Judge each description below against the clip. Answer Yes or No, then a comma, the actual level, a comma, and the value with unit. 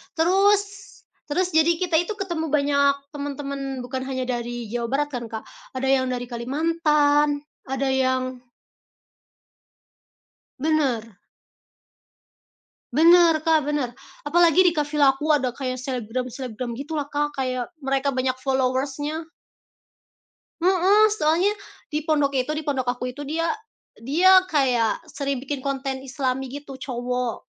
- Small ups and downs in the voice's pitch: No, average, 3.3 semitones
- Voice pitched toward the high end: Yes, very high, 275 Hz